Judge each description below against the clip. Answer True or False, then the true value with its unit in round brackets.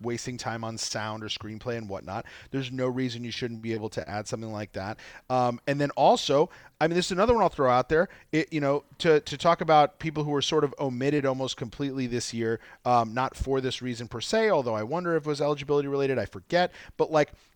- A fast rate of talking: True (240 wpm)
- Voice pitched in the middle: False (130 Hz)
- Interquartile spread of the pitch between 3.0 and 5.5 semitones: True (4.4 semitones)